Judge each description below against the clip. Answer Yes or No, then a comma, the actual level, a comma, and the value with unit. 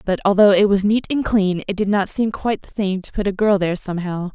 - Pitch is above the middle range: Yes, high, 200 Hz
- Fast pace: Yes, fast, 275 wpm